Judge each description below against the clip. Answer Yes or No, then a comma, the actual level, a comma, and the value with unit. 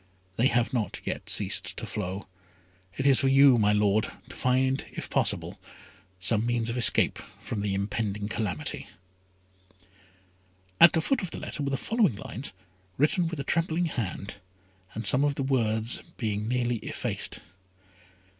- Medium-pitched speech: No, low, 120 Hz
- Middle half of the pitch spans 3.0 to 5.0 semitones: Yes, average, 4.6 semitones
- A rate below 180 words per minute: Yes, average, 155 wpm